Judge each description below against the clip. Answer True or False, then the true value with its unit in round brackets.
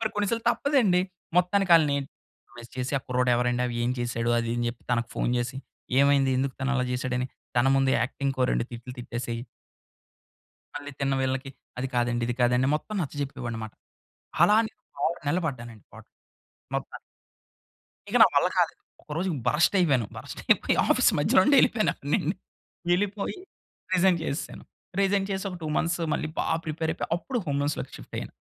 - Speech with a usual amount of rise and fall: False (6.3 semitones)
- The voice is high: False (135 Hz)